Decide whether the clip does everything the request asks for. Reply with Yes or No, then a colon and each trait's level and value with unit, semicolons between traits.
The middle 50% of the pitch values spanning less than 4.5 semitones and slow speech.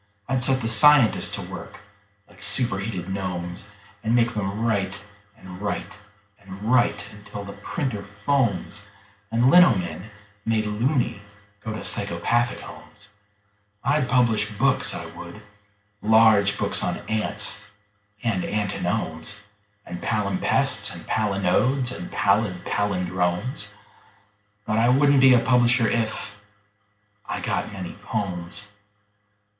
Yes: average, 3.3 semitones; slow, 120 wpm